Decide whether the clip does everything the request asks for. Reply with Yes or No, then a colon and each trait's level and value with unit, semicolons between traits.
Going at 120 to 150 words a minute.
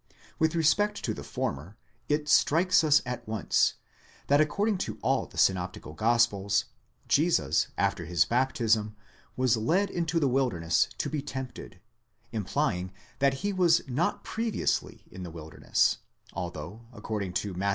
Yes: average, 140 wpm